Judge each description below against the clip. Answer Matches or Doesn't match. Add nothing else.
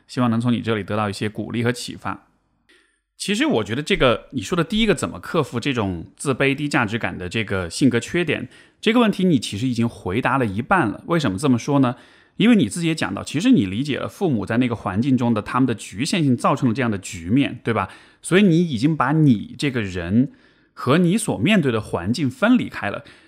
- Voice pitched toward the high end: Doesn't match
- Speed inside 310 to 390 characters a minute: Matches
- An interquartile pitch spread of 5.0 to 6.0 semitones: Matches